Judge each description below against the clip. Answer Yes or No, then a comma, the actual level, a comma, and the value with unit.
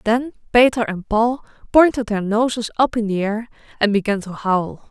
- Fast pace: No, average, 185 wpm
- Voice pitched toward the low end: No, high, 220 Hz